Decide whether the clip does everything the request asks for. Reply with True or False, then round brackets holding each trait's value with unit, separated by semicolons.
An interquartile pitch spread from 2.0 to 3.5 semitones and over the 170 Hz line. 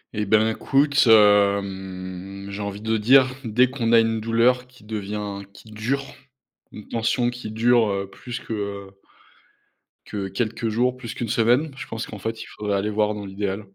False (2.9 semitones; 110 Hz)